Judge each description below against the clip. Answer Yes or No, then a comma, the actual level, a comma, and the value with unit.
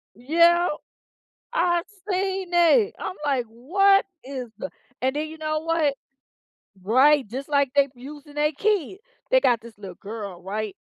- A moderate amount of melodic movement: No, wide, 5.9 semitones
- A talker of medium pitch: No, very high, 290 Hz